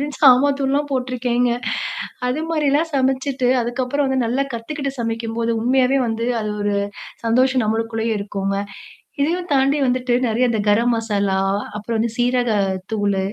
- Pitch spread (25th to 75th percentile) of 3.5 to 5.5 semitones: No, average, 2.9 semitones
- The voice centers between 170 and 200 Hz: No, high, 245 Hz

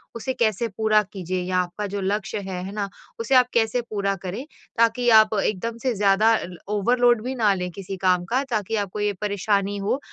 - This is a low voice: No, high, 210 Hz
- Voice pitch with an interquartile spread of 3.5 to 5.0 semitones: No, average, 2.9 semitones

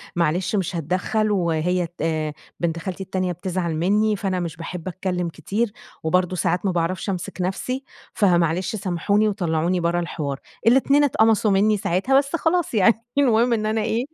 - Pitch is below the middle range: No, medium, 185 Hz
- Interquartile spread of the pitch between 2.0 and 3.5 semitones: No, average, 4.0 semitones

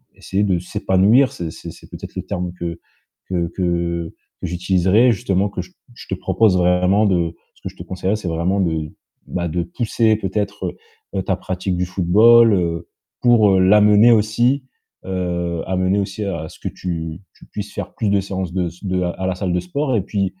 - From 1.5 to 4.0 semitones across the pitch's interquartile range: Yes, average, 2.8 semitones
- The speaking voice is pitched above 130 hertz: No, very low, 95 Hz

